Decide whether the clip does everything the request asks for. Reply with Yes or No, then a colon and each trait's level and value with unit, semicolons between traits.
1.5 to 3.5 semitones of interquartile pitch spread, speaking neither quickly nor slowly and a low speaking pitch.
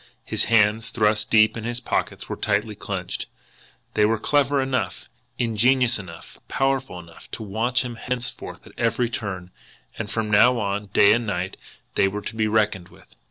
Yes: average, 2.9 semitones; average, 170 wpm; low, 110 Hz